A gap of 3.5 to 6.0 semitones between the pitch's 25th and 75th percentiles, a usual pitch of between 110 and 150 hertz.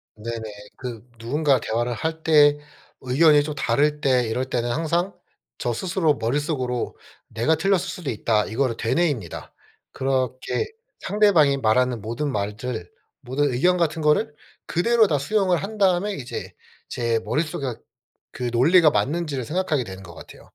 Yes: wide, 5.5 semitones; medium, 140 Hz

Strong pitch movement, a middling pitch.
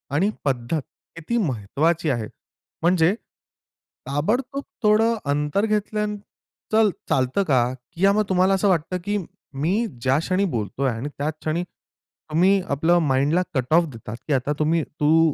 Yes: wide, 5.7 semitones; medium, 160 Hz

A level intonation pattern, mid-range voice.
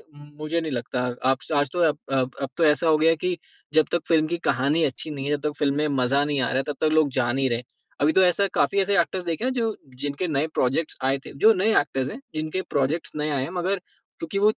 No: average, 3.7 semitones; medium, 150 Hz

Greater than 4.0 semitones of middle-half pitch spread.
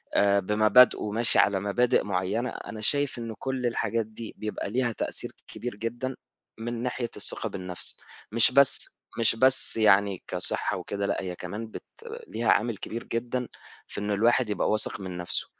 No: average, 2.9 semitones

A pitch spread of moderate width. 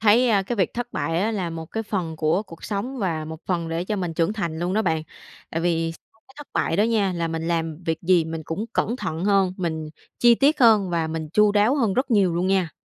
Yes: average, 4.5 semitones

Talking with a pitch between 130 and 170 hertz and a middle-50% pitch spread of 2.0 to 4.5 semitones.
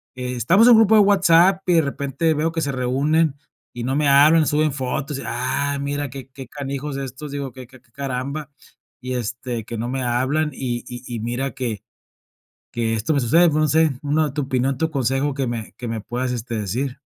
Yes: low, 135 Hz; average, 3.4 semitones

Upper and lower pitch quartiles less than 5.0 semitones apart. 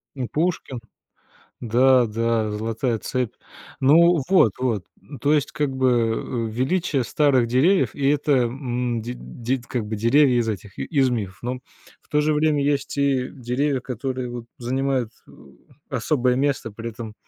Yes: average, 3.2 semitones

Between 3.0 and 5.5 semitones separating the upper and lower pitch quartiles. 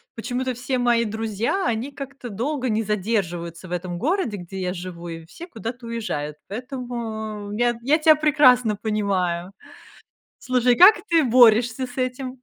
Yes: average, 4.0 semitones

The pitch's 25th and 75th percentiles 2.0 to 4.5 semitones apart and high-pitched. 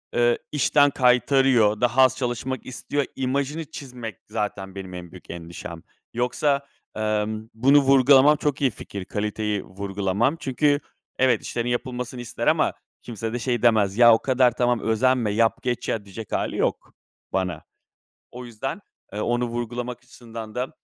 No: average, 3.5 semitones; low, 120 Hz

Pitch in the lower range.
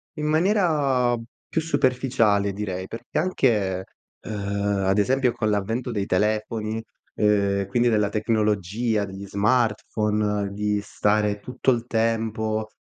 Yes: low, 110 Hz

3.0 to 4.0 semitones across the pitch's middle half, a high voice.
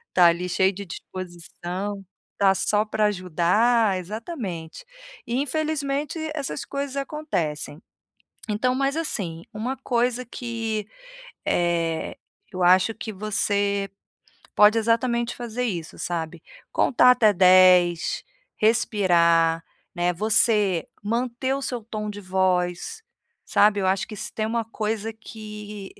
No: average, 4.5 semitones; high, 210 Hz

